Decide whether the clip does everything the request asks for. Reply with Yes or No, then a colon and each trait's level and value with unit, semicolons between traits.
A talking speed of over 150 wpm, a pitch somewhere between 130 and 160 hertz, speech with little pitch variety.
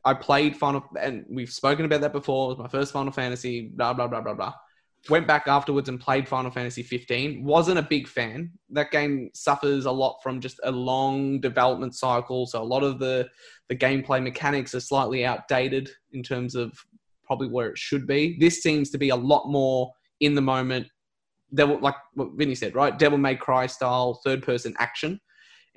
Yes: average, 200 wpm; low, 135 Hz; narrow, 2.1 semitones